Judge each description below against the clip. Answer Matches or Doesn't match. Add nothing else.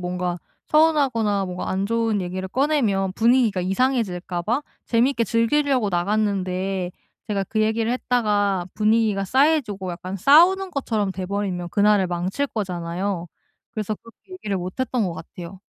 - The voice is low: Doesn't match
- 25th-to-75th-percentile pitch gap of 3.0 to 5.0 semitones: Matches